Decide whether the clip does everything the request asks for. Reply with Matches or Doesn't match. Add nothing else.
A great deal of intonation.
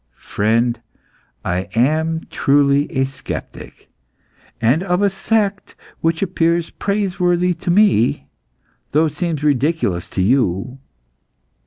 Matches